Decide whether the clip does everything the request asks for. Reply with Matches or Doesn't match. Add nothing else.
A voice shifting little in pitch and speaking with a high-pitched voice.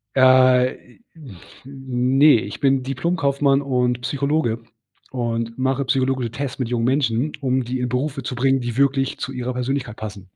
Doesn't match